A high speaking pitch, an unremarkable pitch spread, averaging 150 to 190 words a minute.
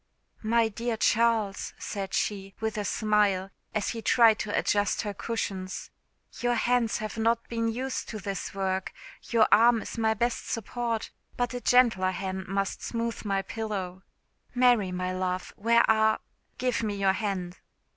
Yes: high, 215 Hz; average, 3.0 semitones; average, 155 wpm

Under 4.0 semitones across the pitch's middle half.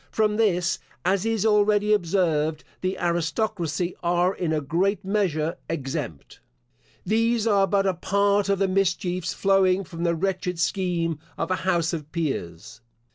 Yes: average, 3.1 semitones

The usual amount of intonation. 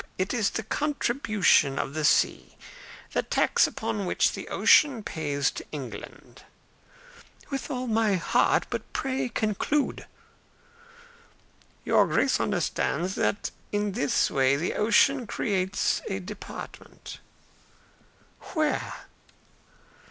No: wide, 5.8 semitones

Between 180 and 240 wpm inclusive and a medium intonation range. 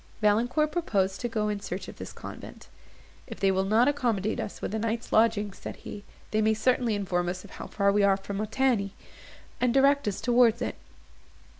Yes: average, 190 wpm; average, 3.3 semitones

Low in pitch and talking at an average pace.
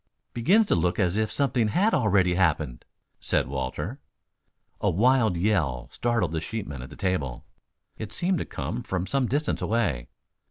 Yes: low, 100 Hz; average, 160 wpm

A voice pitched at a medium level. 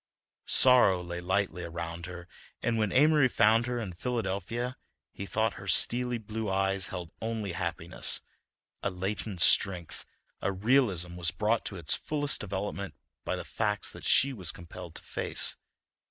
No: low, 100 Hz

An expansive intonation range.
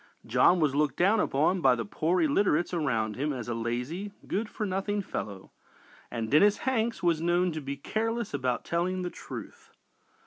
Yes: wide, 6.7 semitones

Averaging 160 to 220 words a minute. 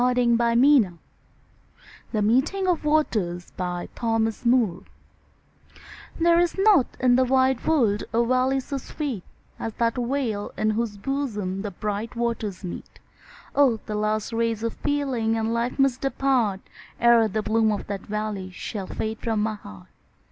No: average, 140 wpm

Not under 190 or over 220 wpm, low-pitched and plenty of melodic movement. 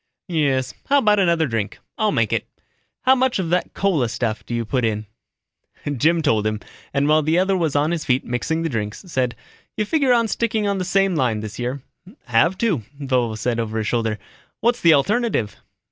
No: average, 200 wpm; medium, 150 Hz; wide, 8.6 semitones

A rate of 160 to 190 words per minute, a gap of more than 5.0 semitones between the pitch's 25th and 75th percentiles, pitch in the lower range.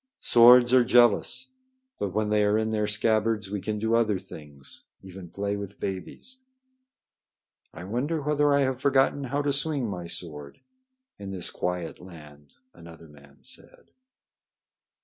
No: average, 150 wpm; wide, 5.6 semitones; low, 105 Hz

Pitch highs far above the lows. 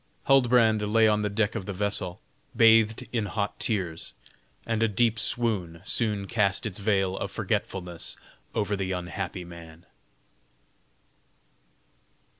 No: average, 3.1 semitones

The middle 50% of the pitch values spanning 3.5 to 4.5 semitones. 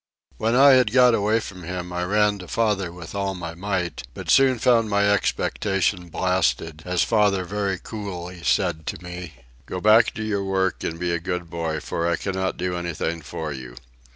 No: average, 3.1 semitones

